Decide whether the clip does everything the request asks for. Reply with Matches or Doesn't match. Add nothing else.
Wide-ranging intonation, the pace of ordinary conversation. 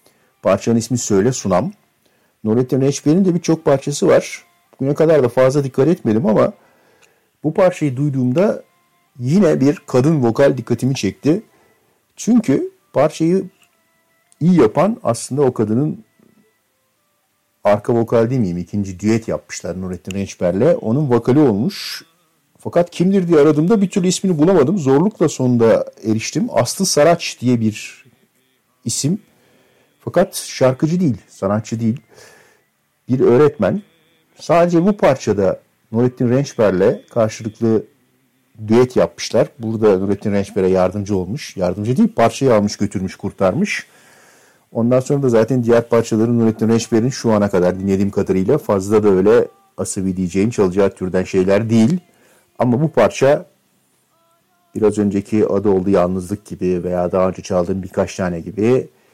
Matches